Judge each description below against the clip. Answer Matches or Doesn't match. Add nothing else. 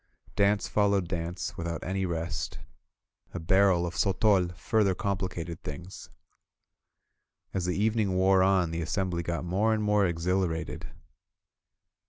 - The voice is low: Matches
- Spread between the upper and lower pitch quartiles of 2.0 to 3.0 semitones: Matches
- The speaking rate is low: Matches